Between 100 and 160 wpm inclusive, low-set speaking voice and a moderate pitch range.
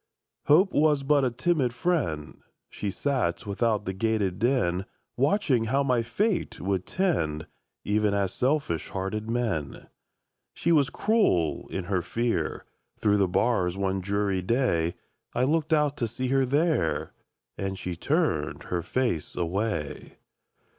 No: average, 140 wpm; low, 115 Hz; wide, 6.7 semitones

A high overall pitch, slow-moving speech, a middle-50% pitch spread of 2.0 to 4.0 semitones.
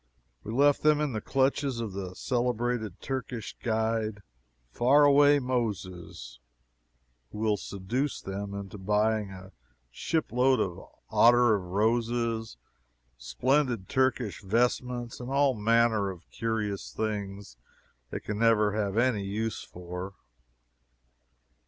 No: low, 110 Hz; slow, 120 wpm; average, 3.7 semitones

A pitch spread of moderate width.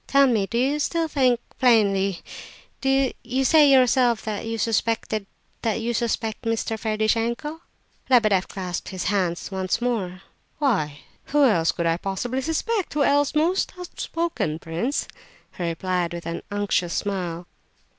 No: wide, 6.0 semitones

